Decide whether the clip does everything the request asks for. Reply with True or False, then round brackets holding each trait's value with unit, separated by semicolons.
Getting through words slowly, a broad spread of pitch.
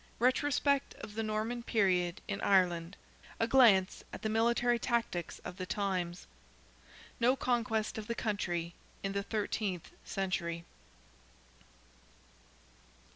False (105 wpm; 4.3 semitones)